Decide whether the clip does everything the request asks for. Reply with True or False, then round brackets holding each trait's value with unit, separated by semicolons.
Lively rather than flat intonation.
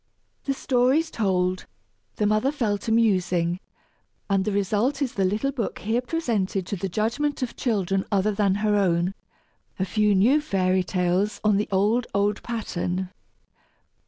False (3.6 semitones)